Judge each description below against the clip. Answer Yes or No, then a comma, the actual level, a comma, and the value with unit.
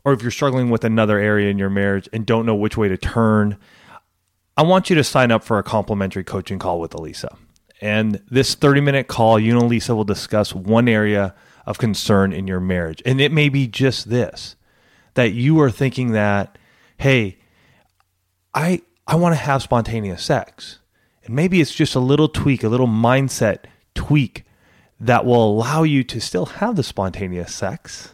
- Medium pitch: No, low, 115 Hz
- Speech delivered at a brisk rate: No, average, 180 wpm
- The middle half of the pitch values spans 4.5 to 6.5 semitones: Yes, average, 4.8 semitones